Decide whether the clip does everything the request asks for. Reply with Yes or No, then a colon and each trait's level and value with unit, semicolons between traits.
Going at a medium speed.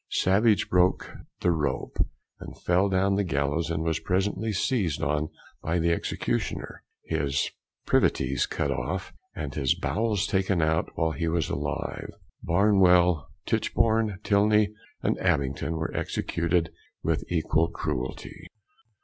No: slow, 130 wpm